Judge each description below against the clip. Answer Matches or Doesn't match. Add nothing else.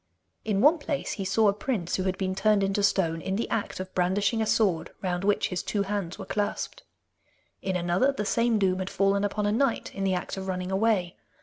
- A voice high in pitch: Matches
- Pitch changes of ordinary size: Doesn't match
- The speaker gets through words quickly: Matches